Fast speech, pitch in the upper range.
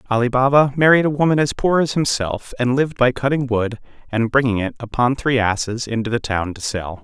No: fast, 215 wpm; low, 125 Hz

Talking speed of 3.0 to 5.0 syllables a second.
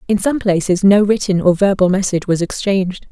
No: 5.8 syllables/s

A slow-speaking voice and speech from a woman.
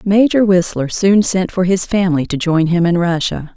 No: average, 200 wpm; female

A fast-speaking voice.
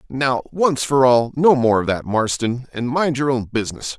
Yes: fast, 210 wpm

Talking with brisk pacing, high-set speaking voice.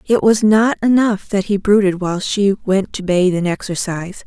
No: average, 195 wpm; high, 200 Hz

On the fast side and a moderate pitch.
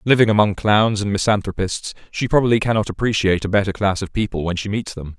No: fast, 210 wpm; low, 105 Hz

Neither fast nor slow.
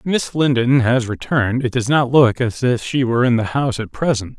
No: fast, 245 wpm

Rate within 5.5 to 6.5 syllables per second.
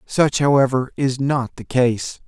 No: 4.0 syllables/s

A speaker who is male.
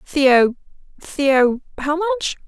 No: female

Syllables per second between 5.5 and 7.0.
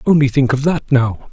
No: 5.2 syllables/s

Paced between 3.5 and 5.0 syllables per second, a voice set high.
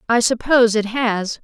Yes: 4.8 syllables/s; high, 230 Hz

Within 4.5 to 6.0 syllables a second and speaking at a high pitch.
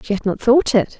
Yes: 5.6 syllables/s; high, 225 Hz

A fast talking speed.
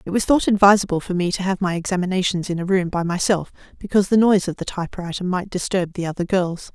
Yes: fast, 230 wpm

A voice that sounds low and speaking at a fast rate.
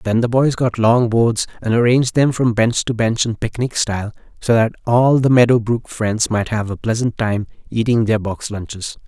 Yes: low, 115 Hz; fast, 210 wpm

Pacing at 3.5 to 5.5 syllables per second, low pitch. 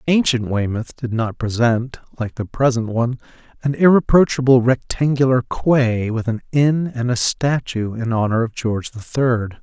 Yes: 4.7 syllables/s; low, 125 Hz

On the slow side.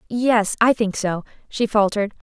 Yes: slow, 130 wpm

